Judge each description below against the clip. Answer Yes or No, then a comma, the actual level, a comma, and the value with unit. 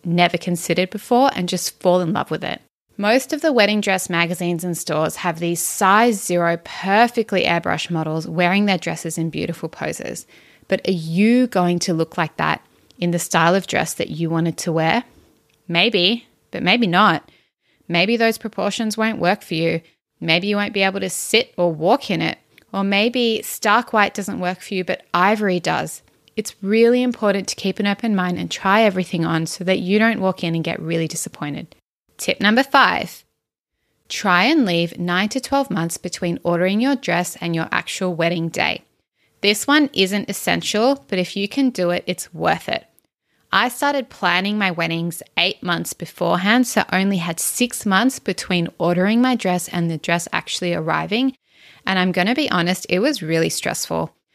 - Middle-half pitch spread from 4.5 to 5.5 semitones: No, average, 3.9 semitones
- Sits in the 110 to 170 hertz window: No, medium, 185 Hz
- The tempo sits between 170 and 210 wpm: Yes, average, 185 wpm